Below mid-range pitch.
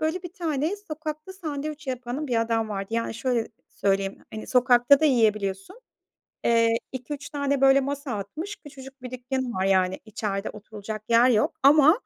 No: very high, 255 Hz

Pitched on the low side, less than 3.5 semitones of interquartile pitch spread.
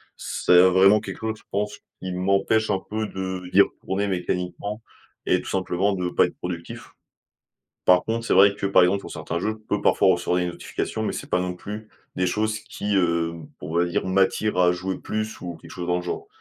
Yes: very low, 95 Hz; narrow, 2.5 semitones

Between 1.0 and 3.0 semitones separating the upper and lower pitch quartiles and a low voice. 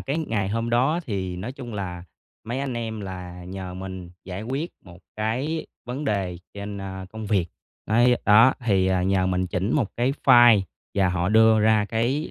No: average, 4.3 semitones; low, 105 Hz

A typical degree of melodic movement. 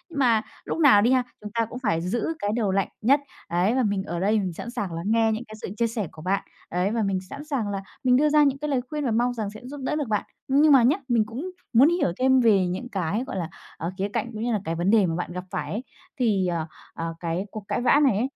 Yes: average, 4.8 semitones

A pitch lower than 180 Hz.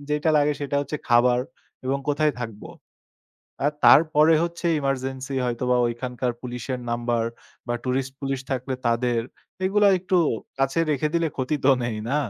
Yes: low, 135 Hz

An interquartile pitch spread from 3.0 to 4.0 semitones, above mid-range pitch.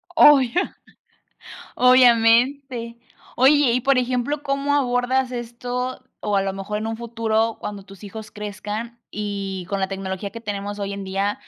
Yes: average, 3.7 semitones; high, 230 Hz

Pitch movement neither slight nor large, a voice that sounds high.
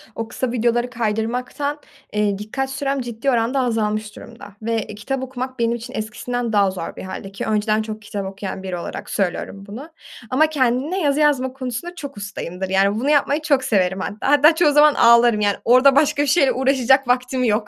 Yes: average, 4.3 semitones; high, 240 Hz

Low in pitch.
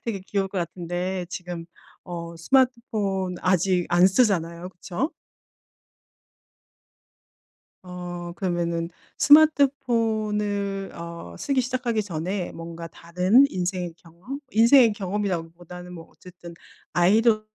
No: medium, 185 Hz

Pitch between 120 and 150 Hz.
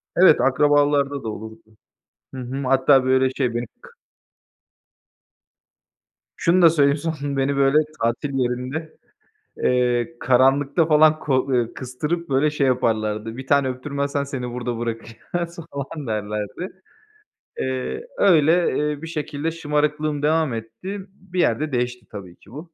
Yes: medium, 140 Hz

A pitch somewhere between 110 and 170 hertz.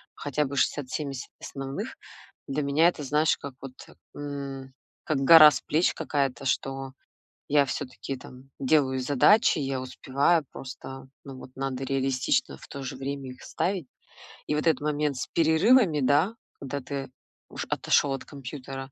Yes: medium, 140 Hz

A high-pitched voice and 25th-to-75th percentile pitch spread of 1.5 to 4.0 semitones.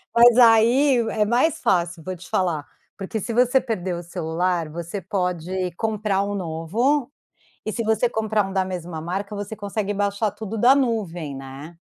No: high, 200 Hz; average, 4.4 semitones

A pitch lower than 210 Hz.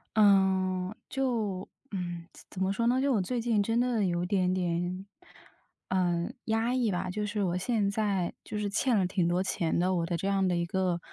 Yes: high, 190 Hz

